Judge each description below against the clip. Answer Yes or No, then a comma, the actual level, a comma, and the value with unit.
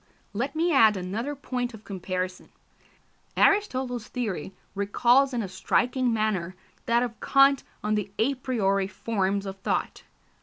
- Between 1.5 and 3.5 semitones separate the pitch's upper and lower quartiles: No, average, 4.6 semitones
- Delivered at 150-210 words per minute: No, average, 140 wpm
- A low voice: No, high, 225 Hz